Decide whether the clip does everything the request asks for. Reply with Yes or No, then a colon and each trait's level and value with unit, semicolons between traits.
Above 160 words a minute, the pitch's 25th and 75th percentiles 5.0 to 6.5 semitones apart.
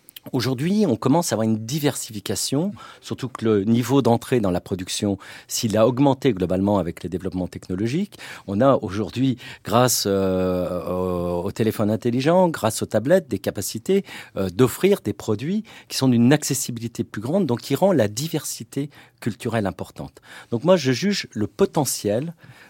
No: average, 155 wpm; wide, 5.5 semitones